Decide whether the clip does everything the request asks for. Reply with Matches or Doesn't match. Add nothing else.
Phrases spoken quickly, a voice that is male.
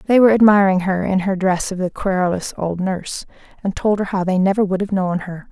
Doesn't match